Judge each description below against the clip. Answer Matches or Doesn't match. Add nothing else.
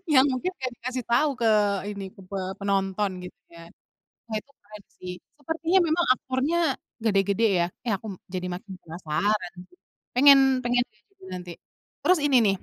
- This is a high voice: Matches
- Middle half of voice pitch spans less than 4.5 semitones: Doesn't match